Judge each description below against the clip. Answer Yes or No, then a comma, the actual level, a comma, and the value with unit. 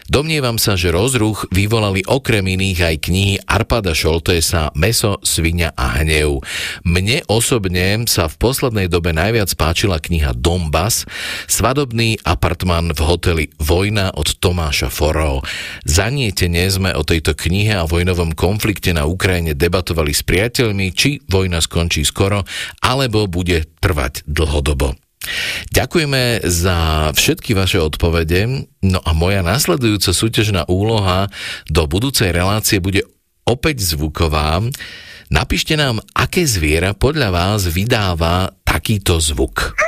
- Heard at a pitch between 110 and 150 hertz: No, very low, 95 Hz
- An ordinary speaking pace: Yes, average, 120 wpm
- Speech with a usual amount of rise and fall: Yes, average, 4.4 semitones